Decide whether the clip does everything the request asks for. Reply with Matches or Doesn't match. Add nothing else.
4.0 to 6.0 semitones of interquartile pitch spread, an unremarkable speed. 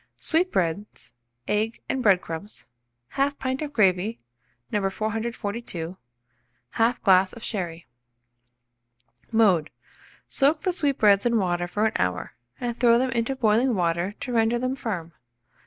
Doesn't match